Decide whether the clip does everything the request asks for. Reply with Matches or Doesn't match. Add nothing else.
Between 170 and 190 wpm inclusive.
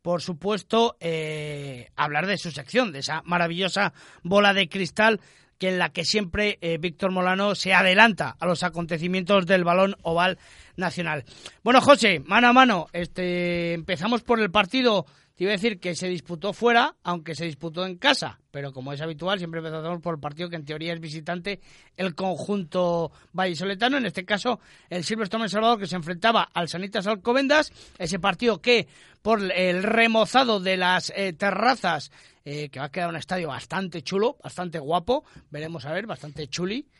Matches